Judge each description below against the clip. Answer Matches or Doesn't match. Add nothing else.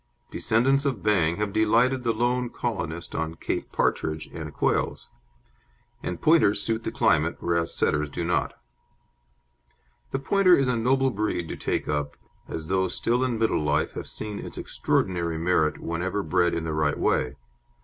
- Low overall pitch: Matches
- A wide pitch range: Matches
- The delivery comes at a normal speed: Matches